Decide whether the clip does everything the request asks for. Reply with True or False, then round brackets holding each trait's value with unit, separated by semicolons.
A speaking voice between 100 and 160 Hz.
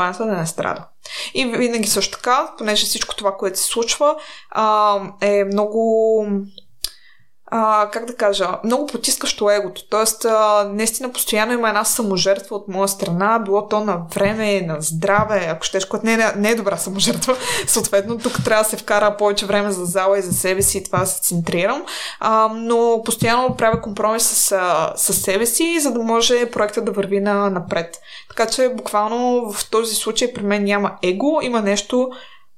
False (215 Hz)